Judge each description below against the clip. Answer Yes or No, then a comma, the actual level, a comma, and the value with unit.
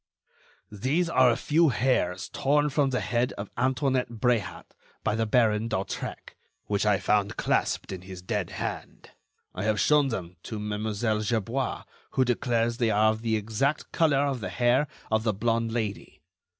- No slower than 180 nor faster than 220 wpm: No, average, 165 wpm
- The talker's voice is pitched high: No, low, 115 Hz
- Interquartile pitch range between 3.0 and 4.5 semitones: Yes, average, 3.7 semitones